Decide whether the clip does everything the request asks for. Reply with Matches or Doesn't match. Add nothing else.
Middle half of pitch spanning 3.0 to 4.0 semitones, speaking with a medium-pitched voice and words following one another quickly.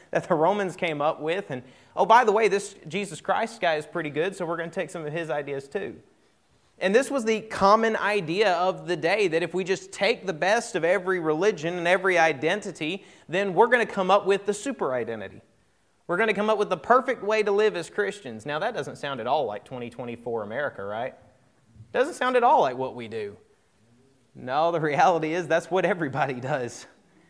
Doesn't match